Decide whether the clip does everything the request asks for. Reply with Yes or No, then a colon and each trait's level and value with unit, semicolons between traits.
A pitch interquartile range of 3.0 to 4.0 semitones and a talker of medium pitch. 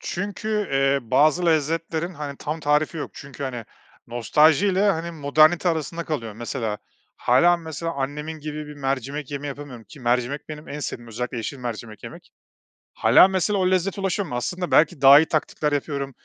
Yes: average, 3.6 semitones; medium, 150 Hz